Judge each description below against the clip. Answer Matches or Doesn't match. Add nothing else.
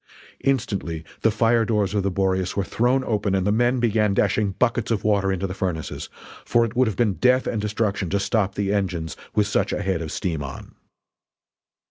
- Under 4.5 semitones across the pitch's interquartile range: Matches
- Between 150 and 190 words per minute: Doesn't match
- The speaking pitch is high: Doesn't match